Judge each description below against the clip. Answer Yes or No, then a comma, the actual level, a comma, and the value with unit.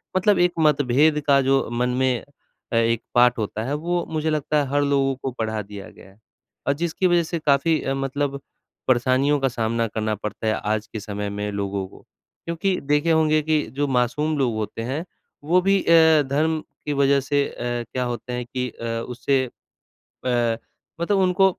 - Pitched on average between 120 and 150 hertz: Yes, low, 135 Hz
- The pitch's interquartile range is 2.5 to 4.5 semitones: No, average, 4.9 semitones